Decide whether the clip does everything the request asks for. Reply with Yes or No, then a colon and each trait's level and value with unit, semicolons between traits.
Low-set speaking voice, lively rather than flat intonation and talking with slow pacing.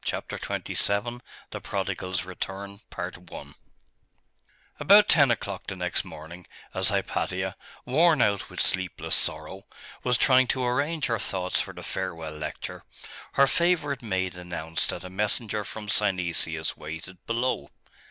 Yes: low, 100 Hz; wide, 5.7 semitones; slow, 130 wpm